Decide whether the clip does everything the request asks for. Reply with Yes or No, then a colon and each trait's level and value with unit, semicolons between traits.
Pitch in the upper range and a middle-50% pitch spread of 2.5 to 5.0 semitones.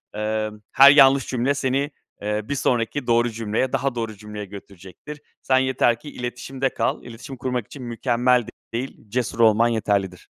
No: low, 120 Hz; average, 3.3 semitones